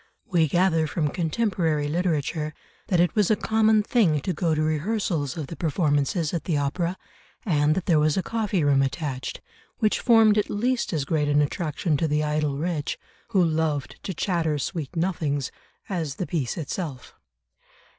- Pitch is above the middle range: No, medium, 160 Hz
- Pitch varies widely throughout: No, average, 4.0 semitones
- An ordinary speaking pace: Yes, average, 170 wpm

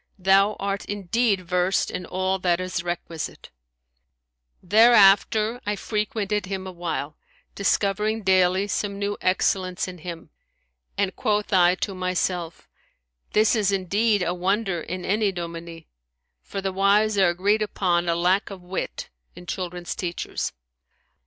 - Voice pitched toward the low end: No, high, 190 Hz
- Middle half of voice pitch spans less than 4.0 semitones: Yes, narrow, 2.5 semitones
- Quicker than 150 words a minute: No, slow, 135 wpm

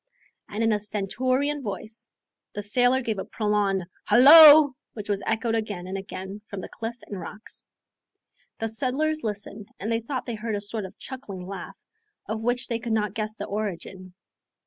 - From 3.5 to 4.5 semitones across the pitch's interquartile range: No, average, 3.1 semitones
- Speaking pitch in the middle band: No, high, 215 Hz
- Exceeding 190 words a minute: No, average, 175 wpm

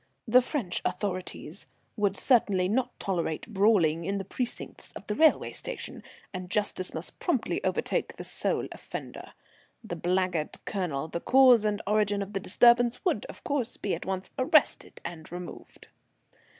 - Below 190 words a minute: Yes, average, 150 wpm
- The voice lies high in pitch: Yes, high, 200 Hz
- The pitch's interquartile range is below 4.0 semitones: No, average, 4.6 semitones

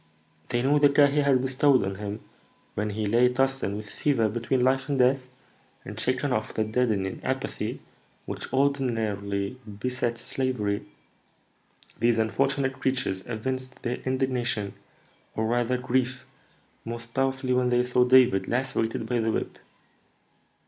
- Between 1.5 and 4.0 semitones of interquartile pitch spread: Yes, average, 3.1 semitones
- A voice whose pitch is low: Yes, low, 125 Hz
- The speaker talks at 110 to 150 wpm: Yes, average, 140 wpm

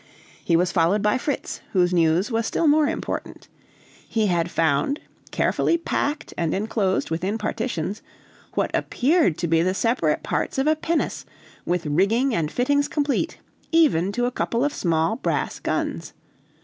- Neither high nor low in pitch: No, high, 210 Hz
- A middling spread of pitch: No, wide, 8.1 semitones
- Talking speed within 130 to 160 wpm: Yes, average, 155 wpm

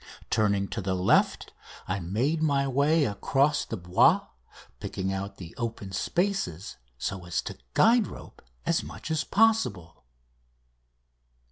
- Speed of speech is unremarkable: No, slow, 130 wpm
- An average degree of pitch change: No, wide, 8.2 semitones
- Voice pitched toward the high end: No, low, 105 Hz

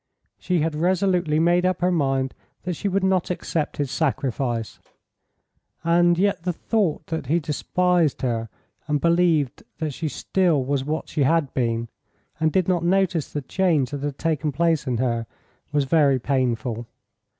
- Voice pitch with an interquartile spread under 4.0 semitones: No, average, 4.5 semitones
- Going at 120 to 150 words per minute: No, average, 160 wpm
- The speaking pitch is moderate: Yes, medium, 155 Hz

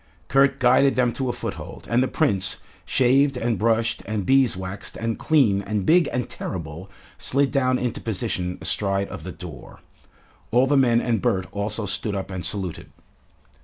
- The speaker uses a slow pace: No, average, 165 wpm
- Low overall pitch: Yes, low, 115 Hz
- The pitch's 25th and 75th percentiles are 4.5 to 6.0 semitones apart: Yes, average, 4.8 semitones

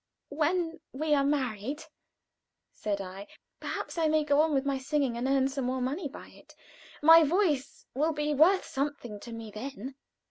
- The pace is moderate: Yes, average, 175 wpm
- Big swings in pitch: No, average, 3.2 semitones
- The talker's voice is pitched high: Yes, very high, 280 Hz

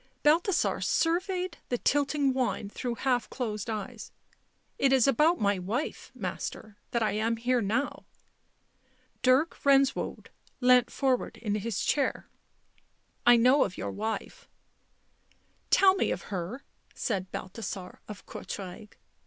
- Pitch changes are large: No, average, 4.7 semitones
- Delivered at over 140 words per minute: No, slow, 135 wpm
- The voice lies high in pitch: Yes, high, 245 Hz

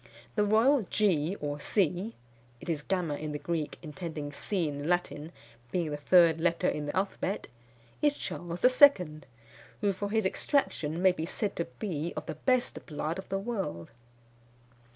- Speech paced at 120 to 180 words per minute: Yes, average, 170 wpm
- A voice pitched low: No, medium, 175 Hz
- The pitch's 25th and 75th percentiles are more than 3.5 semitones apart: Yes, average, 4.9 semitones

